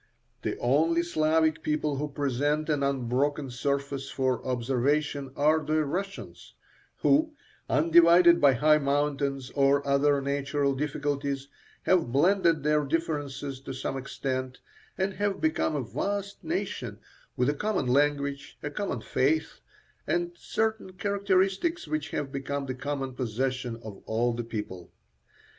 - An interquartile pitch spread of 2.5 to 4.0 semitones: Yes, average, 3.2 semitones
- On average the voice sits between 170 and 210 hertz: No, medium, 145 Hz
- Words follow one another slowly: Yes, slow, 130 wpm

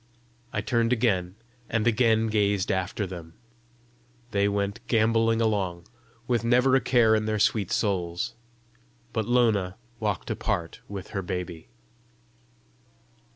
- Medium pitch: No, low, 105 Hz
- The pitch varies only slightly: No, average, 3.3 semitones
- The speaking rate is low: Yes, slow, 120 wpm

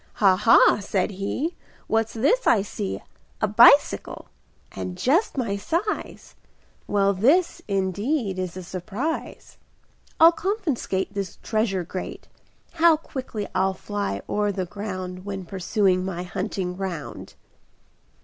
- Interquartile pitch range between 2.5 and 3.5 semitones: No, average, 4.5 semitones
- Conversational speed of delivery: No, slow, 125 wpm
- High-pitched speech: Yes, high, 200 Hz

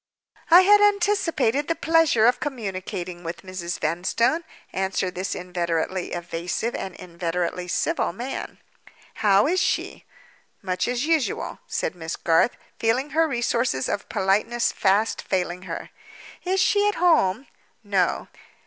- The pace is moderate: No, slow, 130 wpm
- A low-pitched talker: No, high, 200 Hz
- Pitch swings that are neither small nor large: No, wide, 8.3 semitones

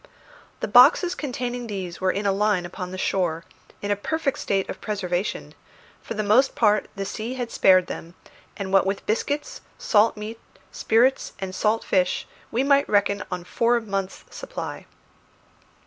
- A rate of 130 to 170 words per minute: Yes, average, 165 wpm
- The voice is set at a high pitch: Yes, high, 205 Hz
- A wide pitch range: No, average, 3.9 semitones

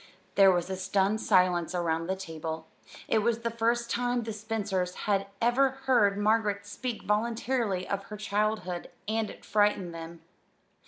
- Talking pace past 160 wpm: No, average, 155 wpm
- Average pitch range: Yes, average, 3.5 semitones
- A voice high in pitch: Yes, high, 205 Hz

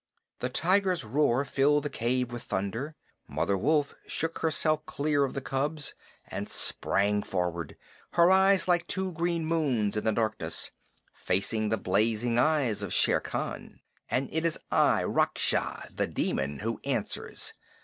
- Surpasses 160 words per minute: No, average, 150 wpm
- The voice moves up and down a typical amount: No, wide, 6.5 semitones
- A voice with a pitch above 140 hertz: No, low, 135 Hz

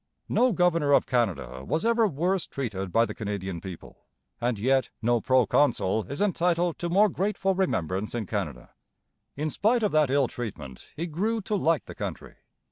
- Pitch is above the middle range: No, medium, 140 Hz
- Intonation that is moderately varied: No, wide, 9.0 semitones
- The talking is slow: No, average, 170 wpm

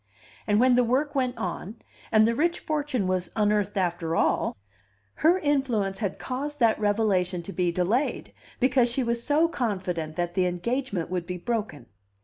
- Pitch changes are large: Yes, wide, 5.9 semitones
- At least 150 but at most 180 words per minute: Yes, average, 165 wpm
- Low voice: No, high, 215 Hz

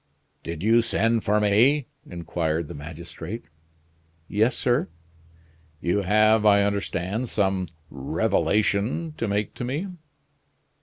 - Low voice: Yes, low, 105 Hz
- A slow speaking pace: Yes, slow, 110 wpm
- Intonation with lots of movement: No, average, 4.5 semitones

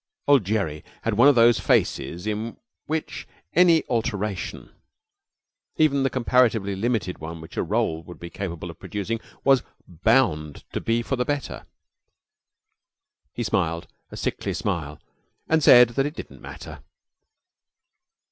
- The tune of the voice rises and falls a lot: Yes, wide, 6.9 semitones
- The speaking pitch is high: No, low, 110 Hz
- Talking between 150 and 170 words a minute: No, average, 140 wpm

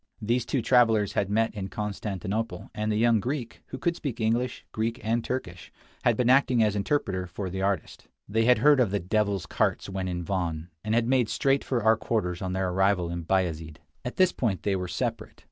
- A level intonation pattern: No, average, 4.0 semitones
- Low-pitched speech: Yes, low, 105 Hz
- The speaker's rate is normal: No, fast, 215 wpm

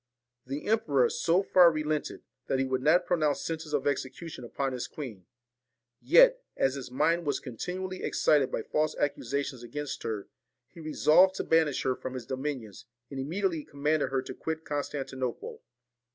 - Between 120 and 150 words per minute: No, average, 160 wpm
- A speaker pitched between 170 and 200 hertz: No, medium, 145 Hz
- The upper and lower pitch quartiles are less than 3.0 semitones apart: No, average, 3.7 semitones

